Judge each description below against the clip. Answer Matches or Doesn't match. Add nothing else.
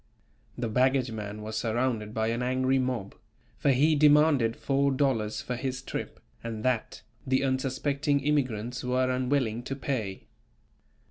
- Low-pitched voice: Matches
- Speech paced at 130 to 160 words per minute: Matches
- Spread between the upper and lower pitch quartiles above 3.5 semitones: Doesn't match